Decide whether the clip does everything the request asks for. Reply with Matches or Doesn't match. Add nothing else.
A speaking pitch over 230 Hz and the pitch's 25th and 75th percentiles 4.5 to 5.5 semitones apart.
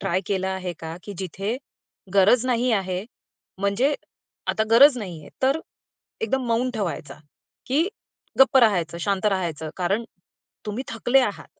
Doesn't match